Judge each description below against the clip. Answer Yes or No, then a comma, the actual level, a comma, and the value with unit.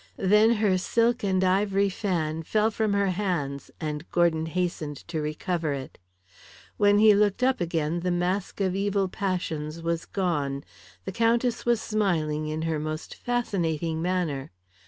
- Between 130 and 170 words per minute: Yes, average, 150 wpm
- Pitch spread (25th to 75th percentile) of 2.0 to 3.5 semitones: No, average, 4.3 semitones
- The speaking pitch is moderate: Yes, medium, 180 Hz